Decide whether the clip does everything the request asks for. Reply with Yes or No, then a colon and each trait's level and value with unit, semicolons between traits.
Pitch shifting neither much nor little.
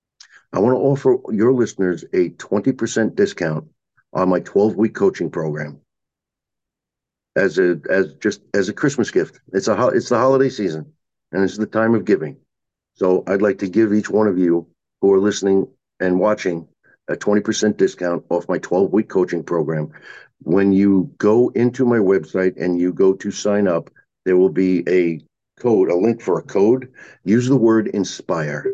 Yes: average, 3.6 semitones